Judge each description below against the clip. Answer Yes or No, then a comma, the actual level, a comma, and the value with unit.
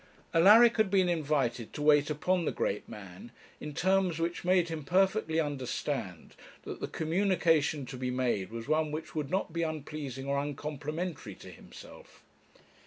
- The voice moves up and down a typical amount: Yes, average, 4.3 semitones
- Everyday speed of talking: Yes, average, 160 wpm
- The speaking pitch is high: No, medium, 155 Hz